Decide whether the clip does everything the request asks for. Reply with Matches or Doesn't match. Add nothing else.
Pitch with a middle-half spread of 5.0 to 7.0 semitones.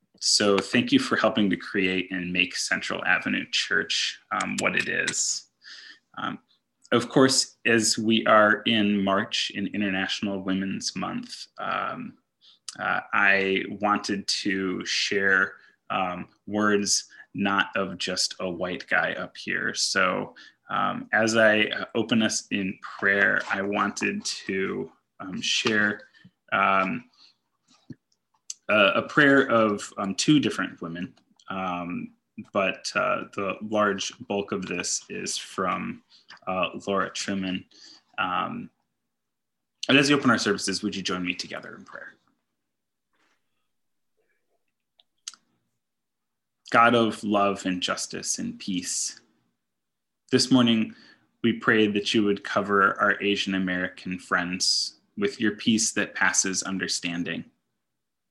Doesn't match